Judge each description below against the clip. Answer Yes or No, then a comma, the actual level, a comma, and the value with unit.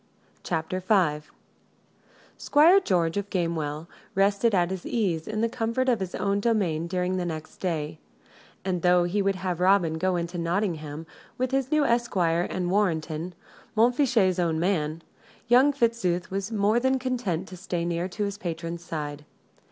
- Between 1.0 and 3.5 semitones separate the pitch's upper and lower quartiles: No, average, 4.3 semitones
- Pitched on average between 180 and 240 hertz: Yes, medium, 185 Hz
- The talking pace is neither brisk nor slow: Yes, average, 160 wpm